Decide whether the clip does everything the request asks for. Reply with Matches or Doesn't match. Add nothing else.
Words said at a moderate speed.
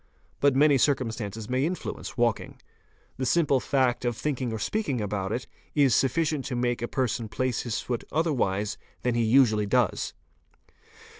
Matches